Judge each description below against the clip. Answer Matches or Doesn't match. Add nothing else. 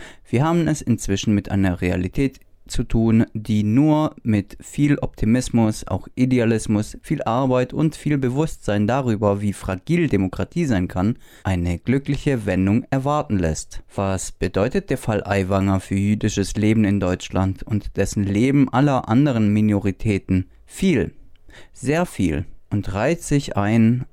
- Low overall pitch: Matches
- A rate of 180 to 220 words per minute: Doesn't match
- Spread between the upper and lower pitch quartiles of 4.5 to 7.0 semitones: Matches